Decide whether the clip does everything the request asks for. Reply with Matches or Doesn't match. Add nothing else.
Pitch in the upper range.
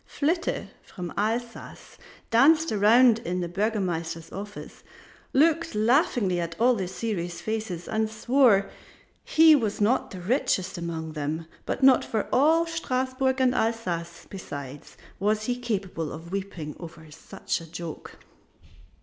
Matches